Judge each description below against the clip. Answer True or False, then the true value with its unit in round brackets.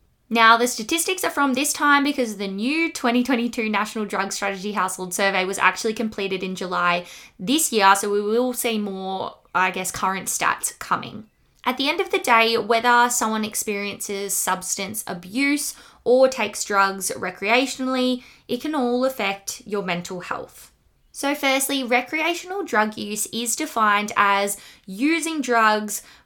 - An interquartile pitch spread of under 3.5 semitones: False (4.5 semitones)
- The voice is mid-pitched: False (220 Hz)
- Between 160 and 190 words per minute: False (150 wpm)